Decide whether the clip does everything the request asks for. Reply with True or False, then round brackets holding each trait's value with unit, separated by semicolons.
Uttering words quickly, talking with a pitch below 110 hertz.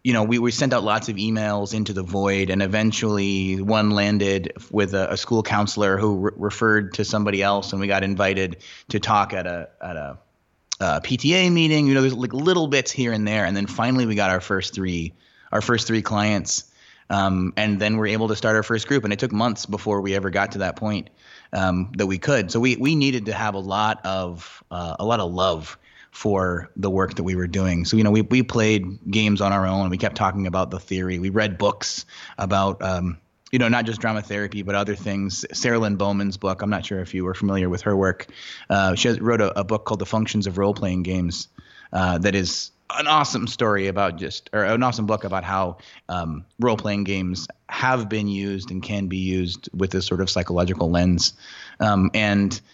True (225 wpm; 100 Hz)